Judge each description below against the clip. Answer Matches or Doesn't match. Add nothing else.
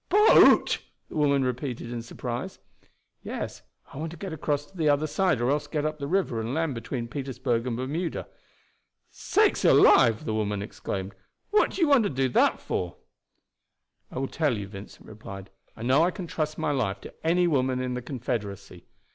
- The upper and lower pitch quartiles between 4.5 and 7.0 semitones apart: Matches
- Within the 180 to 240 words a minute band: Matches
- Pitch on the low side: Matches